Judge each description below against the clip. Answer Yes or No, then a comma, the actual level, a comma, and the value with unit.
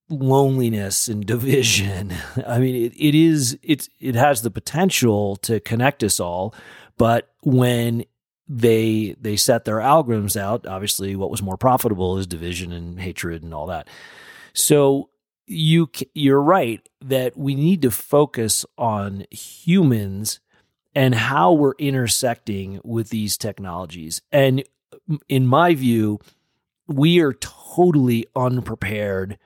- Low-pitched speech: Yes, low, 120 Hz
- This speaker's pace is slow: Yes, slow, 130 wpm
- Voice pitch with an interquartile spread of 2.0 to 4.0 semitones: No, average, 5.3 semitones